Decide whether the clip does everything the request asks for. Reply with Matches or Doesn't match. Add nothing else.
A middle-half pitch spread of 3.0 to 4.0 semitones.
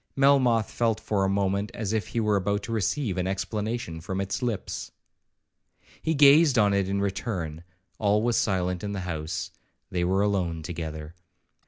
Matches